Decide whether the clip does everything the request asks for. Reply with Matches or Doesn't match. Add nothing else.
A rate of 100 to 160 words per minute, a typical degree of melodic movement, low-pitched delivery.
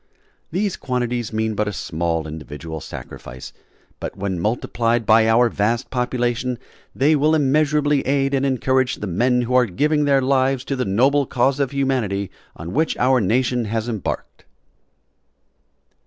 Matches